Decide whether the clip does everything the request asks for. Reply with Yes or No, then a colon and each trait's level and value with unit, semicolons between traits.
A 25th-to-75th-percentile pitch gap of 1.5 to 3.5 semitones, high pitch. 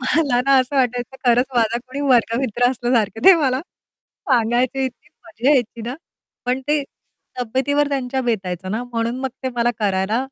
Yes: narrow, 2.4 semitones; high, 245 Hz